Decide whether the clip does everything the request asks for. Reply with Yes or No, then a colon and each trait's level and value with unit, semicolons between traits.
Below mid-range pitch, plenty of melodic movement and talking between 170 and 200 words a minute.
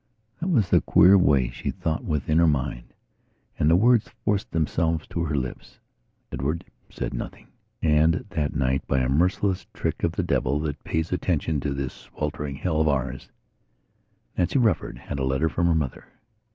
No: very low, 80 Hz; average, 3.9 semitones; average, 175 wpm